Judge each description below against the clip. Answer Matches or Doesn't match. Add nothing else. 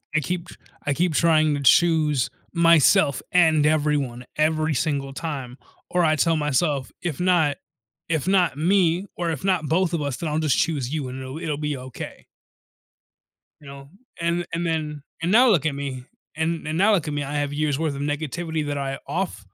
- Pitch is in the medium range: Matches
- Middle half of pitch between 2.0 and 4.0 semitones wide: Matches